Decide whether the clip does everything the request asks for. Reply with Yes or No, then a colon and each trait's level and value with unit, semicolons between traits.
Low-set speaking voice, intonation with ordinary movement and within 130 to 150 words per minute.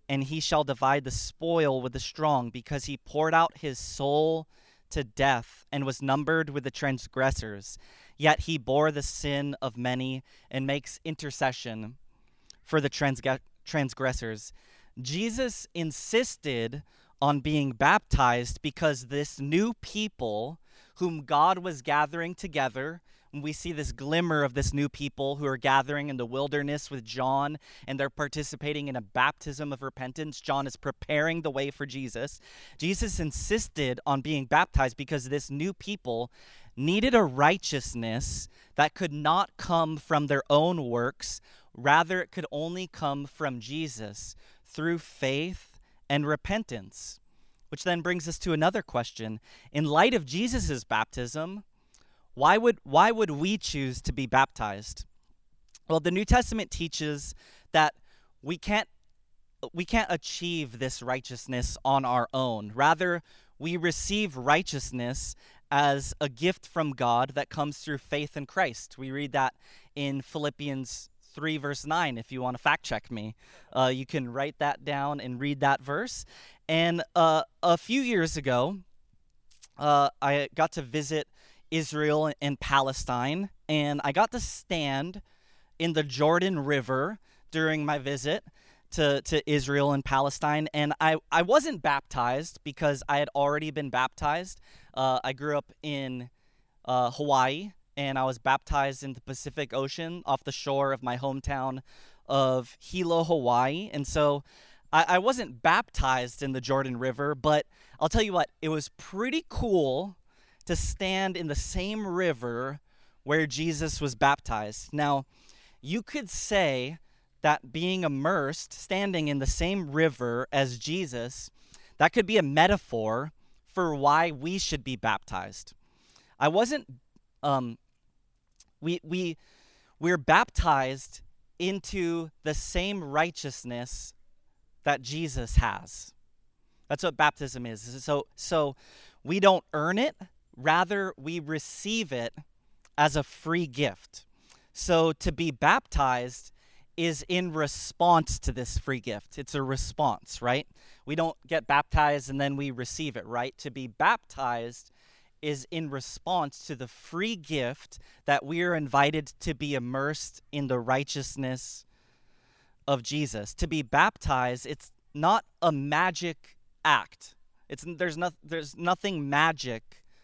No: medium, 145 Hz; average, 3.7 semitones; average, 140 wpm